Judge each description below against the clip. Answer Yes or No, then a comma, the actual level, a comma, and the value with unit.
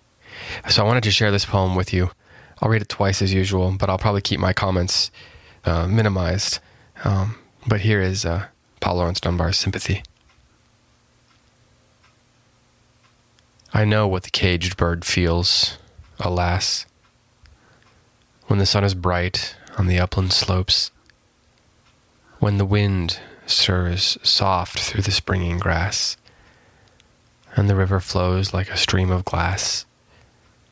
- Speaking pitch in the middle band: No, low, 100 Hz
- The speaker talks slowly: Yes, slow, 130 wpm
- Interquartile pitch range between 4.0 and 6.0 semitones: No, average, 3.0 semitones